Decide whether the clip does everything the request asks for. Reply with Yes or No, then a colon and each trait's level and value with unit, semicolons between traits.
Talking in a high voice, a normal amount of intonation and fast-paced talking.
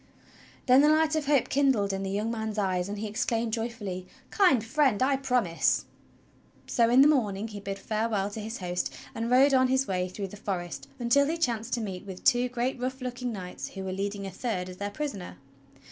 Yes: high, 225 Hz; average, 4.5 semitones; fast, 210 wpm